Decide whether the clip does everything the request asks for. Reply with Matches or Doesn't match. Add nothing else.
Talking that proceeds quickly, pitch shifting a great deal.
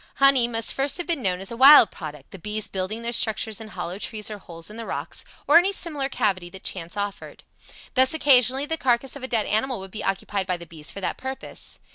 Matches